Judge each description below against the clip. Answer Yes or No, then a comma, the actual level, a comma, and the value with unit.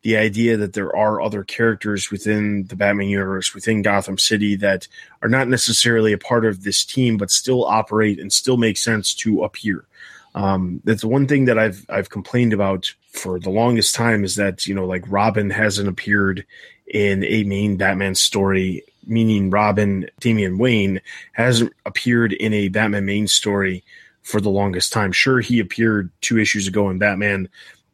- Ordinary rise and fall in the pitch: No, narrow, 2.3 semitones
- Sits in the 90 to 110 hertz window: Yes, low, 105 Hz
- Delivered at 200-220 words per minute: No, average, 170 wpm